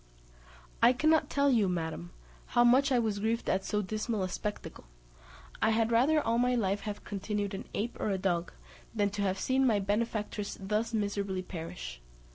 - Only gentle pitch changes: No, average, 3.2 semitones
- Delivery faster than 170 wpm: Yes, average, 180 wpm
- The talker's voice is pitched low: No, high, 210 Hz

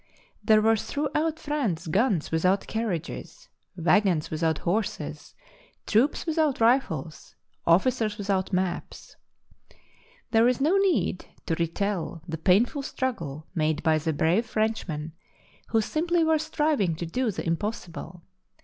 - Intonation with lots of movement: Yes, wide, 7.8 semitones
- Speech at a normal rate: No, slow, 120 wpm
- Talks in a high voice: Yes, high, 205 Hz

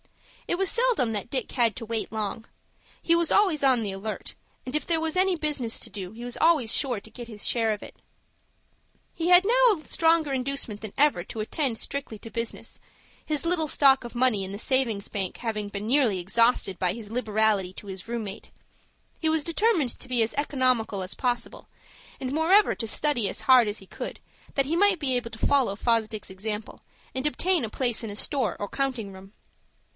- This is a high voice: Yes, high, 240 Hz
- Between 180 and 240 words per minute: Yes, fast, 205 wpm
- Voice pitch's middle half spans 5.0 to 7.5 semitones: Yes, wide, 5.6 semitones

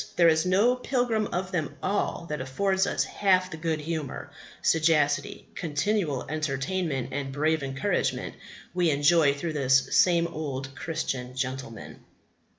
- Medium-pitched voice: Yes, medium, 155 Hz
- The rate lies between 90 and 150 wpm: Yes, slow, 135 wpm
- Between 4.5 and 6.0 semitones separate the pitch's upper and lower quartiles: Yes, average, 4.8 semitones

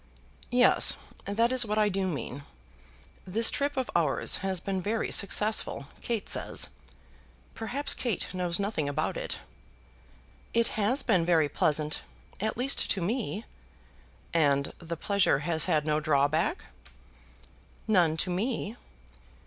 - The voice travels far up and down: Yes, wide, 5.9 semitones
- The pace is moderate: No, slow, 130 wpm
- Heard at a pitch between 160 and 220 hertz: Yes, high, 190 Hz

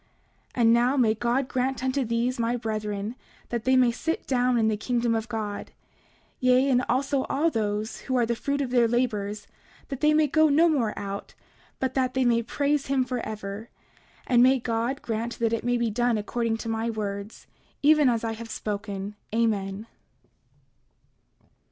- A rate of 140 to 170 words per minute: No, average, 180 wpm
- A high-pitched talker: Yes, high, 235 Hz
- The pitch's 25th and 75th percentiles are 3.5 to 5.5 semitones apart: No, average, 2.8 semitones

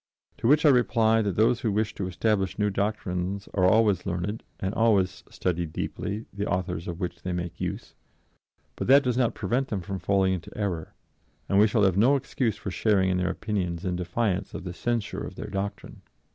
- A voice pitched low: Yes, low, 100 Hz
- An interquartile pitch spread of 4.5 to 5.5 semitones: No, average, 3.1 semitones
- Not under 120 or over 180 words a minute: No, average, 200 wpm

